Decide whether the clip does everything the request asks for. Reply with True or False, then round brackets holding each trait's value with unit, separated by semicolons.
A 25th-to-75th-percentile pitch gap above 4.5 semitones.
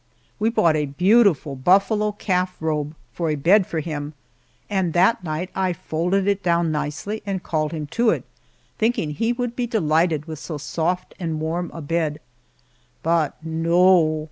False (3.9 semitones)